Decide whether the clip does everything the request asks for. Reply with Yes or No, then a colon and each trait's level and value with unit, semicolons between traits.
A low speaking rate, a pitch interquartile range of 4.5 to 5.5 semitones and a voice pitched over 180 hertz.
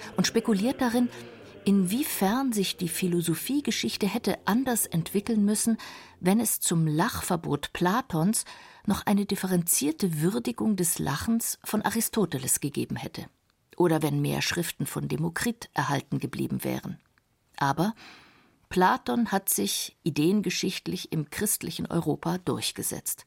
Yes: slow, 115 wpm; average, 5.1 semitones; high, 190 Hz